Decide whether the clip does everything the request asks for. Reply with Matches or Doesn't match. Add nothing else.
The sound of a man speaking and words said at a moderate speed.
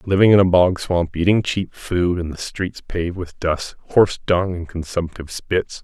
Matches